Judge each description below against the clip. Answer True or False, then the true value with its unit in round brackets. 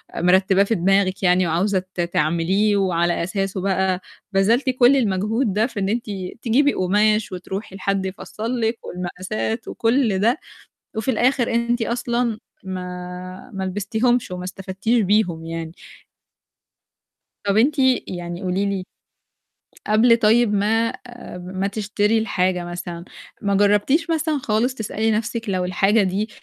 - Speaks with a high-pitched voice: True (200 Hz)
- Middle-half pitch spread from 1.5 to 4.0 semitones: True (3.5 semitones)